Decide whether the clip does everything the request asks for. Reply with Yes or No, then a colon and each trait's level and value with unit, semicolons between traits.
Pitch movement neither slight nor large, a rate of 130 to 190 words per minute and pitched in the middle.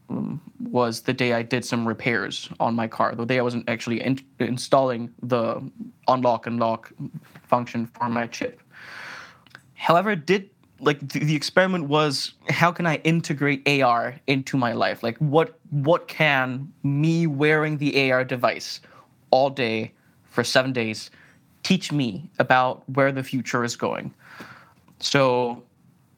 No: average, 4.1 semitones; average, 145 wpm; low, 130 Hz